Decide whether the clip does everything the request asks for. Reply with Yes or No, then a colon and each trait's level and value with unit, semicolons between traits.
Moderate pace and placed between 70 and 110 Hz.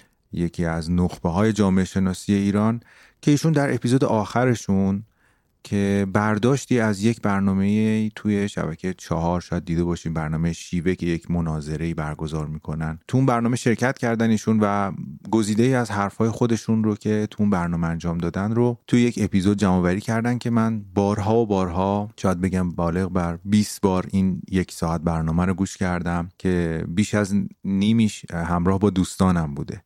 No: fast, 165 wpm; low, 100 Hz